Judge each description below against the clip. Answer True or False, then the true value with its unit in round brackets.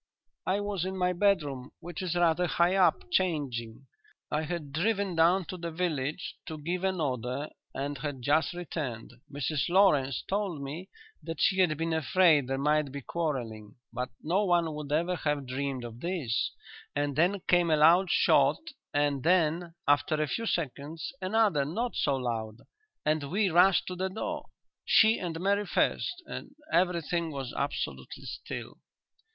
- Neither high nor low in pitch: True (160 Hz)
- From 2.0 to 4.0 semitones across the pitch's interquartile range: False (4.4 semitones)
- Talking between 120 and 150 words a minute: False (160 wpm)